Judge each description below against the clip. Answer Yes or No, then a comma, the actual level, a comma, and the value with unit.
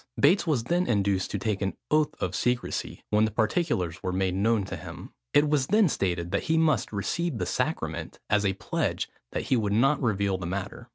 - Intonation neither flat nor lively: No, wide, 7.2 semitones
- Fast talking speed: Yes, fast, 210 wpm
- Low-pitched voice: Yes, low, 110 Hz